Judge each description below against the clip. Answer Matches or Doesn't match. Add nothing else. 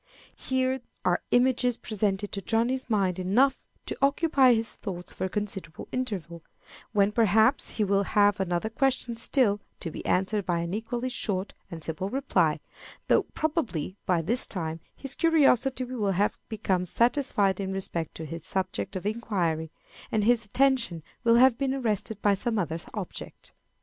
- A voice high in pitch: Matches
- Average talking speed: Matches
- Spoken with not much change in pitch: Doesn't match